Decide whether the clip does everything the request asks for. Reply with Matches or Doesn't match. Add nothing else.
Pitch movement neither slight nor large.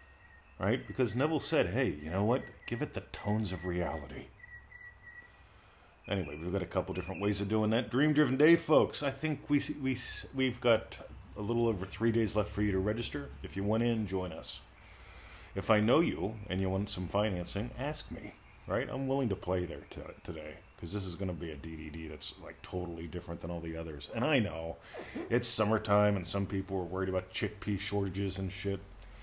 Matches